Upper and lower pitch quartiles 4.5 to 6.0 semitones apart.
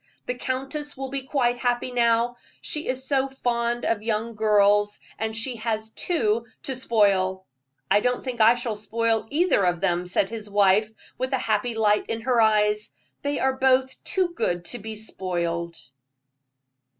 No: average, 3.5 semitones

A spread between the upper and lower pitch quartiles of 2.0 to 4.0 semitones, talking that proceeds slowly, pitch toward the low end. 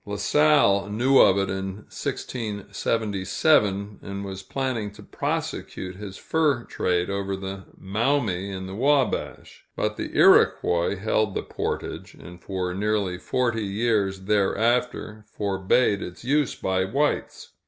Yes: average, 3.5 semitones; slow, 130 wpm; low, 100 Hz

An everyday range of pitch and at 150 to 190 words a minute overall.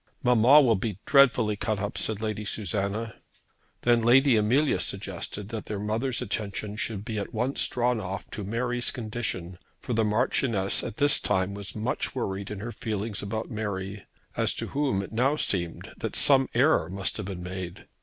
Yes: average, 3.4 semitones; average, 175 wpm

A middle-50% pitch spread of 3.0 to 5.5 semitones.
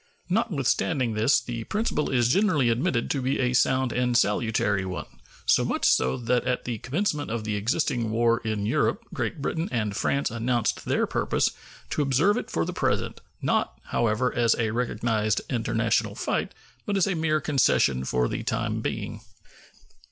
Yes: average, 4.2 semitones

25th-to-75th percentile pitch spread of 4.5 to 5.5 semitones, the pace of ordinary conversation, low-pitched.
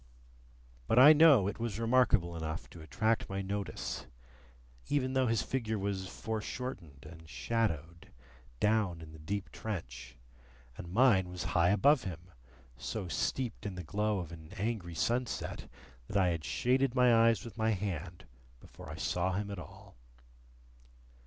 Yes: average, 5.1 semitones; average, 150 wpm; low, 100 Hz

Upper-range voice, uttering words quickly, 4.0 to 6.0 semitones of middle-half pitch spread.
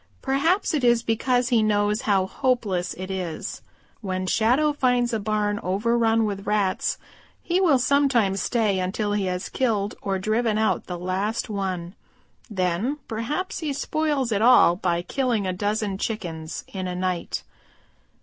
No: high, 215 Hz; average, 150 wpm; average, 4.6 semitones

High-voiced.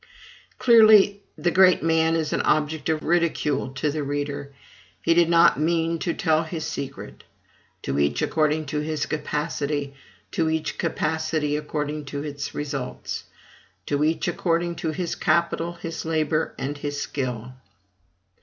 No: medium, 155 Hz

